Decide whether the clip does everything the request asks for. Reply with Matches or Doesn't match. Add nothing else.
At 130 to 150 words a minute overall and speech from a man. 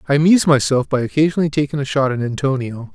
Doesn't match